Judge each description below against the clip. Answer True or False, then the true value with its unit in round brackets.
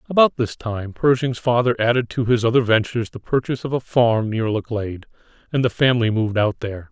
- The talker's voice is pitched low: True (120 Hz)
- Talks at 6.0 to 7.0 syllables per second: True (6.1 syllables/s)